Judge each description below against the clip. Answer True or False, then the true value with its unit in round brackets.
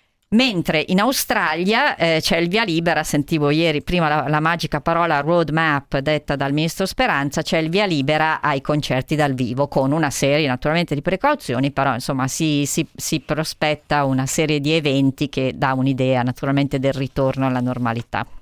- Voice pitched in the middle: True (150 Hz)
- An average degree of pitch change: True (3.2 semitones)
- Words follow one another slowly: False (170 wpm)